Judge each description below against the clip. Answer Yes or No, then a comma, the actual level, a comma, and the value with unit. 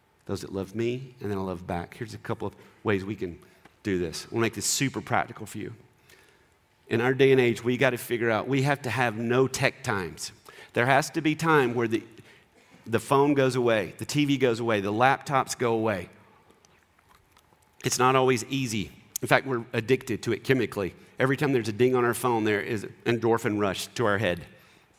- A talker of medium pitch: No, low, 120 Hz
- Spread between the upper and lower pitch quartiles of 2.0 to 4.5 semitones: Yes, average, 3.6 semitones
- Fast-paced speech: Yes, fast, 210 wpm